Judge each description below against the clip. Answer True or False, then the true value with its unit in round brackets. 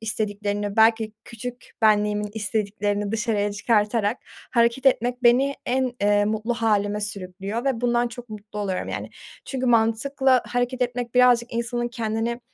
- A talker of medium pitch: False (225 Hz)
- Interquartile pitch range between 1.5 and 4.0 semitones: True (2.7 semitones)